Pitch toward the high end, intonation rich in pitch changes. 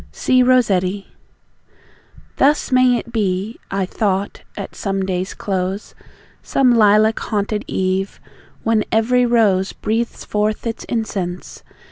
No: high, 210 Hz; average, 3.4 semitones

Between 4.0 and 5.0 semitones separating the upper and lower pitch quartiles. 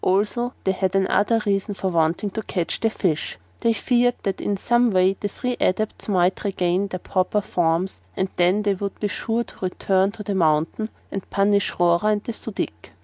No: narrow, 2.4 semitones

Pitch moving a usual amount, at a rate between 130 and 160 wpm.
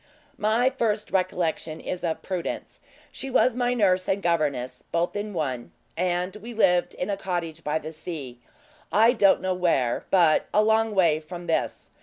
No: average, 4.6 semitones; average, 170 wpm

